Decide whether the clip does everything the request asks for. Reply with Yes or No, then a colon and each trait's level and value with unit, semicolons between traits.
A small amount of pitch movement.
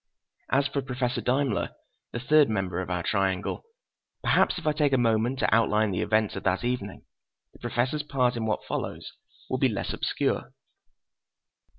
No: average, 4.4 semitones